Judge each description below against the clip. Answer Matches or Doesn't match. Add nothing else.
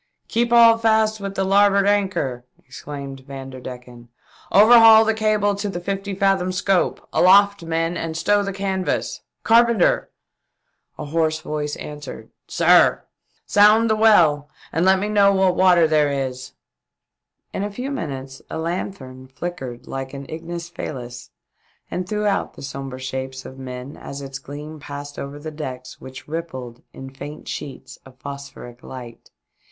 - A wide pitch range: Matches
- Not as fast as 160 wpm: Doesn't match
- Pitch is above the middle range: Doesn't match